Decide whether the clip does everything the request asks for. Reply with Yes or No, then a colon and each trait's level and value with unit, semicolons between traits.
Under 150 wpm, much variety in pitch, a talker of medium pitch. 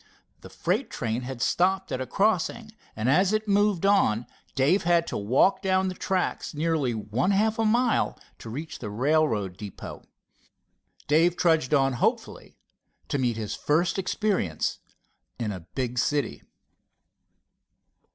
Yes: average, 140 wpm; wide, 7.9 semitones; medium, 155 Hz